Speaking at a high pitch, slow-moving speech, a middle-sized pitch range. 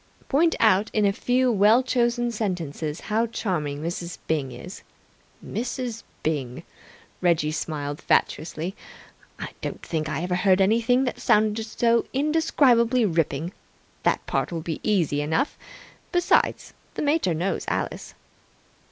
No: high, 195 Hz; slow, 130 wpm; wide, 6.8 semitones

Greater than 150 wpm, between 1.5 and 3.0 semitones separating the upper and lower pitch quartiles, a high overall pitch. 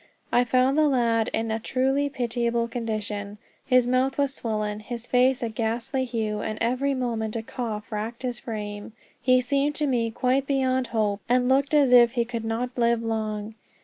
Yes: average, 180 wpm; narrow, 2.6 semitones; high, 240 Hz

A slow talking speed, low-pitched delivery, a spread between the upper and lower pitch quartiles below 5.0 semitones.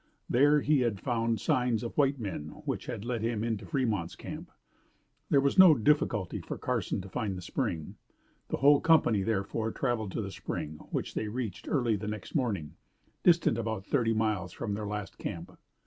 No: average, 180 wpm; low, 115 Hz; average, 4.1 semitones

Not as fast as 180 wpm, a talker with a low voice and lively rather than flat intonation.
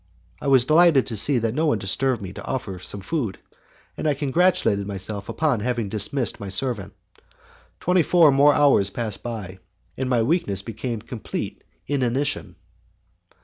Yes: average, 160 wpm; low, 120 Hz; wide, 6.0 semitones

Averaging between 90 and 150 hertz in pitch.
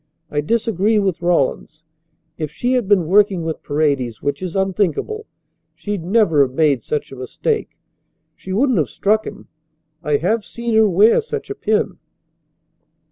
No: high, 190 Hz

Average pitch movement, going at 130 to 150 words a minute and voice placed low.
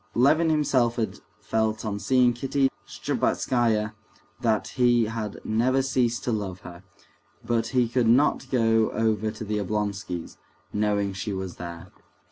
Yes: average, 3.0 semitones; average, 140 wpm; low, 110 Hz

